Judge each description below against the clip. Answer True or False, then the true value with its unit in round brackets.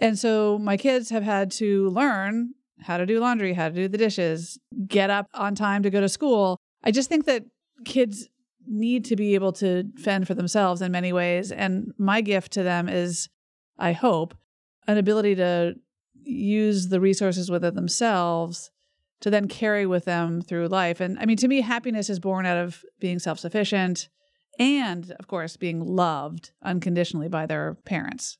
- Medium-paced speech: True (180 wpm)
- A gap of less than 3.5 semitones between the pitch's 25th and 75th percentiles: False (3.9 semitones)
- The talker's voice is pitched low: False (195 Hz)